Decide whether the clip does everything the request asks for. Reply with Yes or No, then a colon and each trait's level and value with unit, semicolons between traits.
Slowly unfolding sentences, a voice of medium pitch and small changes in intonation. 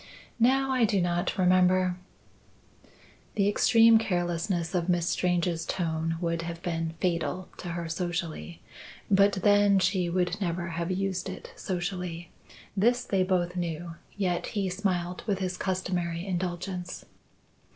Yes: slow, 130 wpm; medium, 180 Hz; narrow, 2.0 semitones